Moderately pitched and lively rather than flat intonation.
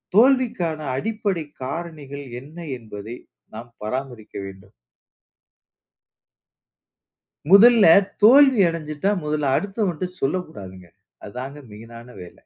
Yes: medium, 150 Hz; wide, 8.9 semitones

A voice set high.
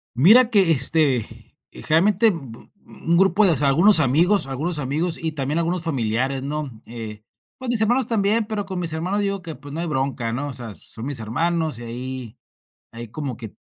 No: medium, 155 Hz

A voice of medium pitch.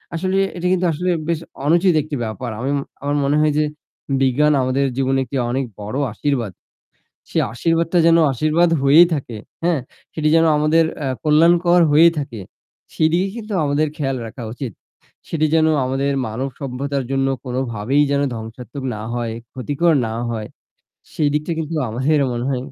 Yes: medium, 145 Hz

